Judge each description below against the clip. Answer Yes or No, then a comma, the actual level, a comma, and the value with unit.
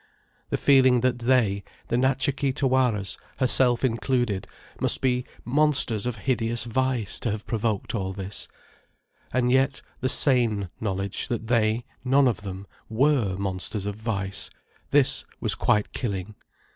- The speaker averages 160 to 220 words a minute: No, average, 140 wpm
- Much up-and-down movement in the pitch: No, average, 4.1 semitones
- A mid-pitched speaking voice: No, low, 120 Hz